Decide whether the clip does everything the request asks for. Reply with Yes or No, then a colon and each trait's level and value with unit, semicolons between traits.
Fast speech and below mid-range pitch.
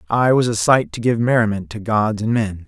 Yes: fast, 245 wpm; low, 110 Hz